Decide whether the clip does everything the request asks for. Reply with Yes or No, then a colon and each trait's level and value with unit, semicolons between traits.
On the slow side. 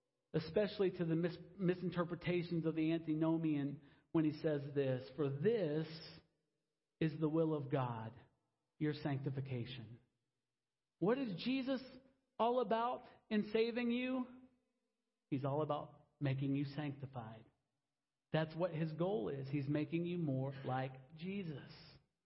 Yes: slow, 125 wpm